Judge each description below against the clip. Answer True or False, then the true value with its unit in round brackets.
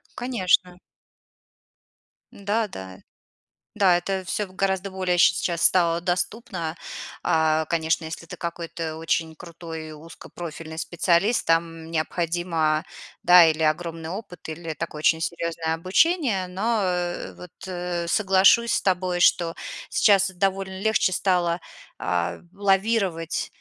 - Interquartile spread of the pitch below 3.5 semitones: True (2.6 semitones)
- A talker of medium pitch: True (175 Hz)